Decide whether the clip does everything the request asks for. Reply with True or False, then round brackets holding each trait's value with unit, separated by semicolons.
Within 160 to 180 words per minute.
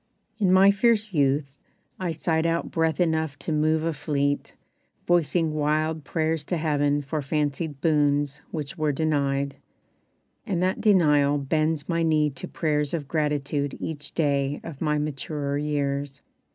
False (145 wpm)